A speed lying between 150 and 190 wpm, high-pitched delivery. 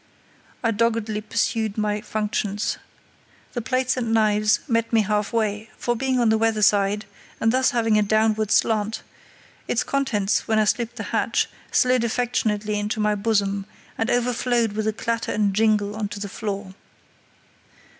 Yes: average, 160 wpm; high, 220 Hz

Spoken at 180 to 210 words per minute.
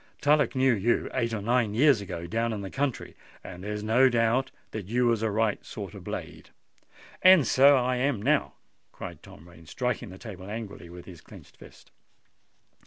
Yes: average, 190 wpm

